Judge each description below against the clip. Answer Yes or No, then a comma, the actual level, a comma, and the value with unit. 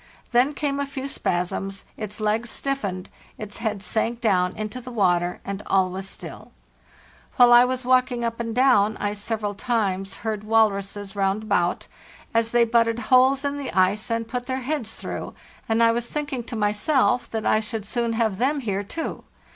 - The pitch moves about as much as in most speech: Yes, average, 3.5 semitones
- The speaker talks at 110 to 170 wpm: No, average, 180 wpm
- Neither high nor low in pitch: No, high, 225 Hz